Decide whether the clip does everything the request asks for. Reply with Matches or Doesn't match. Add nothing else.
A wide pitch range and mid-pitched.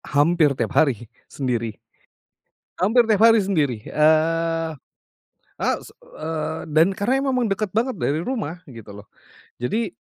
Matches